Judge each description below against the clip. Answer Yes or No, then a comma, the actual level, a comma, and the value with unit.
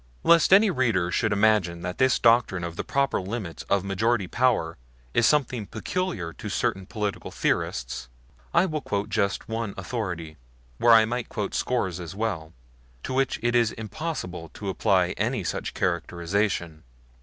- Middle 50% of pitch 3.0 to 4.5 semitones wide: No, average, 5.1 semitones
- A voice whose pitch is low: Yes, low, 105 Hz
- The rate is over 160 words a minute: No, average, 155 wpm